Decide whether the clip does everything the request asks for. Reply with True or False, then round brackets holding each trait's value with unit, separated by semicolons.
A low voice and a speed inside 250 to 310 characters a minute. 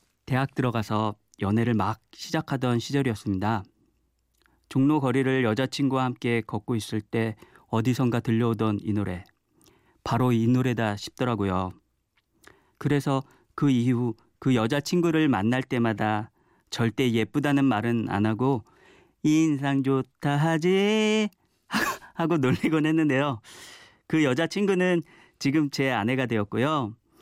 True (125 Hz; 260 characters per minute)